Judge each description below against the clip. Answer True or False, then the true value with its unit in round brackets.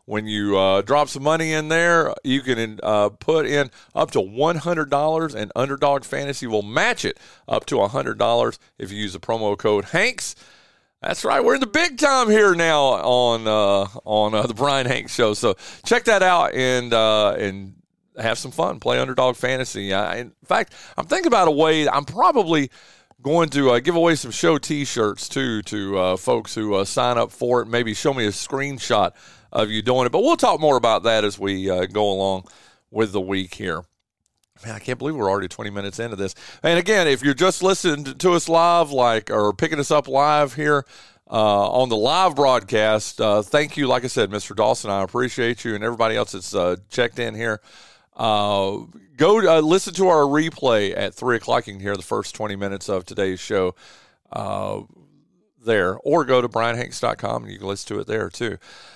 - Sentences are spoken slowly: False (200 wpm)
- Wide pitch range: True (5.8 semitones)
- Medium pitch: False (120 Hz)